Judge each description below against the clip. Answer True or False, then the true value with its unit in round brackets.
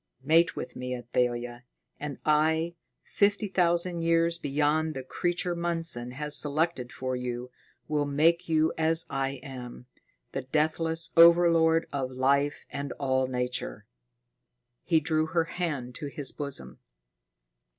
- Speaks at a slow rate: True (130 wpm)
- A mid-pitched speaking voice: True (150 Hz)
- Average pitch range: True (4.2 semitones)